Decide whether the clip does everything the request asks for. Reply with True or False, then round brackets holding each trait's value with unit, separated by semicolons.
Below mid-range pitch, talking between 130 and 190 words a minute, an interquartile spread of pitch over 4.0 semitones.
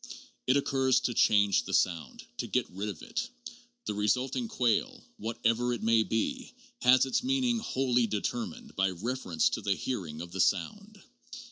True (120 Hz; 160 wpm; 5.6 semitones)